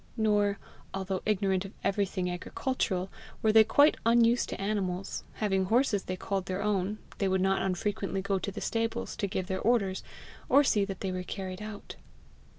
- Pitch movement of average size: No, narrow, 2.3 semitones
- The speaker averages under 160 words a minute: No, average, 175 wpm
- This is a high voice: Yes, high, 195 Hz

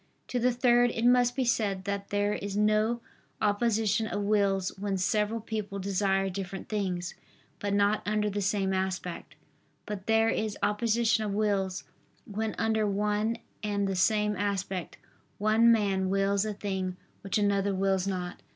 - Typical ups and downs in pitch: No, narrow, 1.9 semitones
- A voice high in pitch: Yes, high, 205 Hz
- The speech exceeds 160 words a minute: No, average, 155 wpm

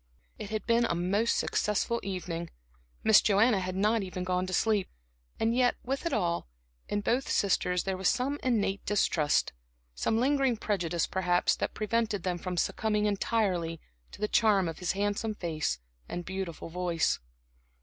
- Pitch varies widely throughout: No, average, 3.6 semitones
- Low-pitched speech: No, high, 200 Hz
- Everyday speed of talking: Yes, average, 160 wpm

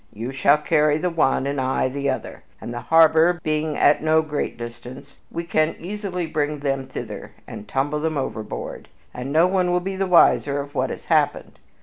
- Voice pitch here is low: No, medium, 150 Hz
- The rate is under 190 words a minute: No, average, 195 wpm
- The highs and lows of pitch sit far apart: No, average, 3.2 semitones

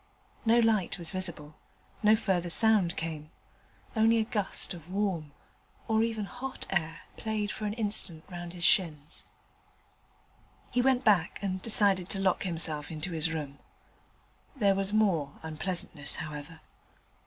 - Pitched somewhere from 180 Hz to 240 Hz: Yes, medium, 185 Hz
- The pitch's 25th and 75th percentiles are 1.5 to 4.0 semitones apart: No, average, 4.8 semitones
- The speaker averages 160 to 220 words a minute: No, average, 140 wpm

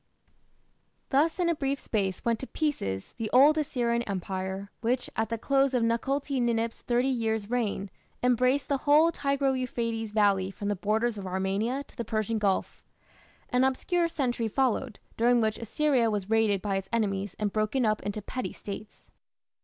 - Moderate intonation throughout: Yes, average, 4.3 semitones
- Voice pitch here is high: Yes, high, 230 Hz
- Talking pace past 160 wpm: Yes, average, 170 wpm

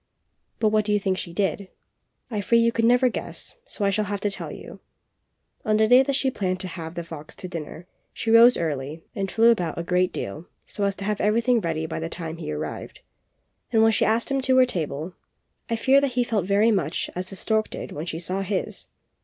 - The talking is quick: Yes, fast, 235 wpm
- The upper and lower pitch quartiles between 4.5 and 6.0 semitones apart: Yes, average, 5.1 semitones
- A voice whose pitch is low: No, high, 200 Hz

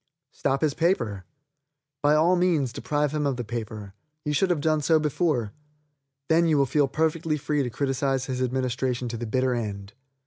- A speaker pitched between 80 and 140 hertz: Yes, low, 135 Hz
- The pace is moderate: Yes, average, 180 wpm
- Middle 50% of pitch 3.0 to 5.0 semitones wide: Yes, average, 4.0 semitones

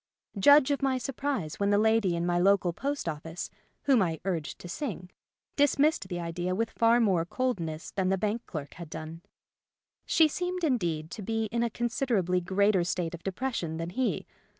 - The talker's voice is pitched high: Yes, high, 195 Hz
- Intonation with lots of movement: Yes, wide, 6.1 semitones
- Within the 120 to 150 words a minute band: No, average, 185 wpm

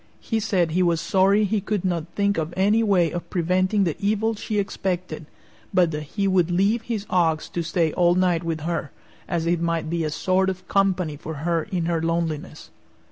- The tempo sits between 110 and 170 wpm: No, average, 200 wpm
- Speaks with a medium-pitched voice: Yes, medium, 175 Hz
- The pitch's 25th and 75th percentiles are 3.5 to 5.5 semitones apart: No, average, 3.0 semitones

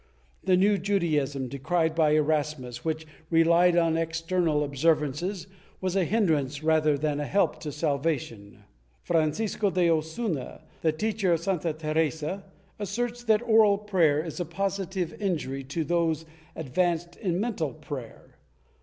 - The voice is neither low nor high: Yes, medium, 165 Hz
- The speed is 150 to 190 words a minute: No, slow, 135 wpm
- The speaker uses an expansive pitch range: No, average, 3.6 semitones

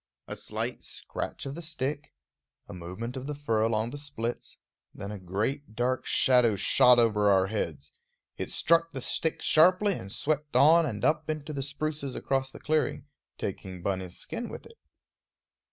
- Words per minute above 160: Yes, average, 170 wpm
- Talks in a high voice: No, low, 130 Hz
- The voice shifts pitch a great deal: Yes, wide, 6.2 semitones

